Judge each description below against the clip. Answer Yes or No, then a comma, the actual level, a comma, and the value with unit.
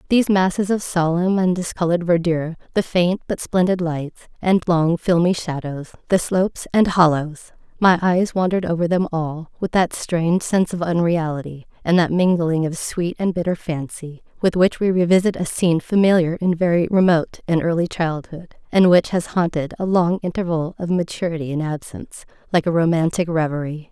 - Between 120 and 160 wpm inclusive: No, average, 170 wpm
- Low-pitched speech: No, medium, 170 Hz